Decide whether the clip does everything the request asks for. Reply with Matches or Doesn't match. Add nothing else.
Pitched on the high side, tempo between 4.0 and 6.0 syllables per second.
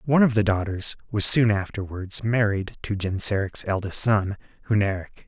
Doesn't match